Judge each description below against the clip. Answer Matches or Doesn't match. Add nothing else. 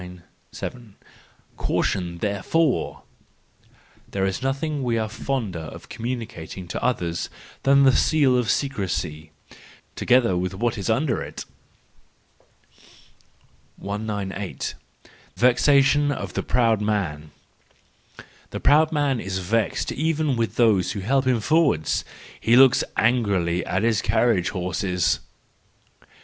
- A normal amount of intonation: Doesn't match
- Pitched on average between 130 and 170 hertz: Doesn't match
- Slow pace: Matches